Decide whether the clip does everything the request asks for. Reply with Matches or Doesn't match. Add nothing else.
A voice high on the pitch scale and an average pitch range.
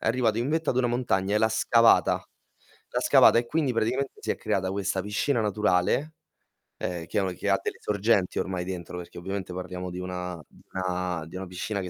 Doesn't match